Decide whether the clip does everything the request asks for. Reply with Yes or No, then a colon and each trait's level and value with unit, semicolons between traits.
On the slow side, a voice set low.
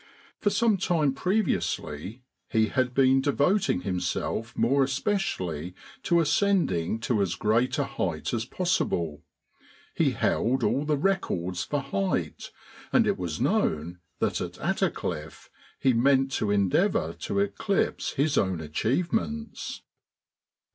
Yes: slow, 125 wpm; low, 130 Hz